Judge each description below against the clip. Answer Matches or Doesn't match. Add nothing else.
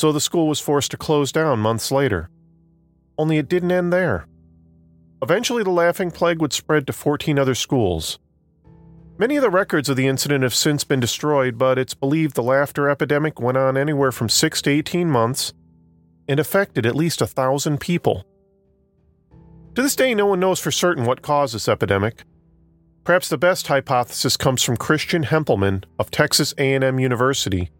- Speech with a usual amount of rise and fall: Doesn't match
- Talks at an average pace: Matches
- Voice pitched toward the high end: Doesn't match